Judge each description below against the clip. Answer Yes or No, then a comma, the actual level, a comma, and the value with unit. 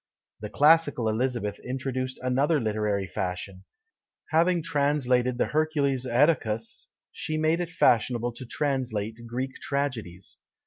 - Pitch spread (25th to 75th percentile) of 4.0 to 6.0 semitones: Yes, average, 4.5 semitones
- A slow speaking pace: Yes, slow, 115 wpm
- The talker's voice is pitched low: Yes, low, 130 Hz